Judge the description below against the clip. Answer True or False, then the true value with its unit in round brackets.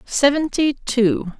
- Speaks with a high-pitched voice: True (250 Hz)